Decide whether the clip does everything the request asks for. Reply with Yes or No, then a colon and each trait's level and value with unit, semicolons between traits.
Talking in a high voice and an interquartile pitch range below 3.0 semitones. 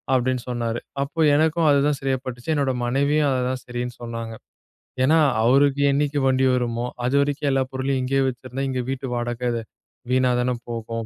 No: low, 130 Hz; narrow, 2.4 semitones